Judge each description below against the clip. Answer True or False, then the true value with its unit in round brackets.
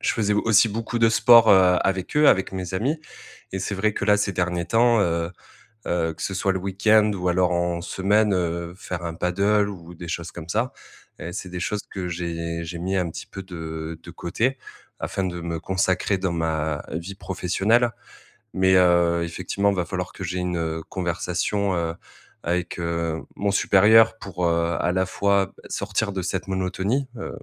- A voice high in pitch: False (90 Hz)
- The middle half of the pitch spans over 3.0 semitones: False (2.7 semitones)